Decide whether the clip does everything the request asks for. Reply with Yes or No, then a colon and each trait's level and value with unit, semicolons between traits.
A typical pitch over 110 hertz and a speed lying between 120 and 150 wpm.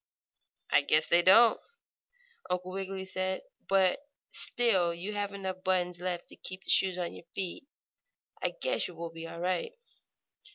No: medium, 185 Hz; average, 160 wpm